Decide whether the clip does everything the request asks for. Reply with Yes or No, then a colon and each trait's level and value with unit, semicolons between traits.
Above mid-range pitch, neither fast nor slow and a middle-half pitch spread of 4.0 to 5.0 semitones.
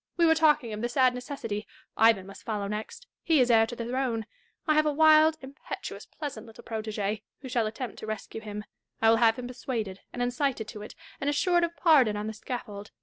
No: high, 240 Hz; fast, 220 wpm; average, 4.7 semitones